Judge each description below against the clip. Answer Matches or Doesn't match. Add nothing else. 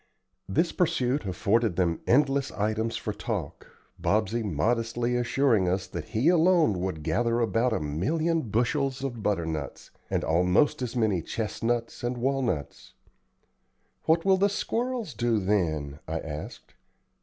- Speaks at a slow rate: Matches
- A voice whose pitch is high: Doesn't match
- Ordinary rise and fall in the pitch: Doesn't match